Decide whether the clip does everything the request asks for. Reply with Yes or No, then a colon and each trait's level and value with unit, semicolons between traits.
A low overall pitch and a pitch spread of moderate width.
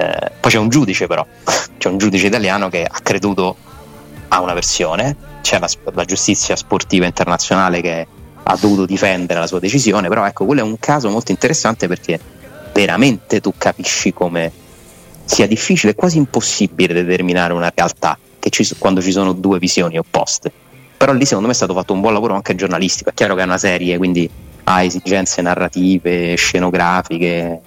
No: very low, 90 Hz; narrow, 2.0 semitones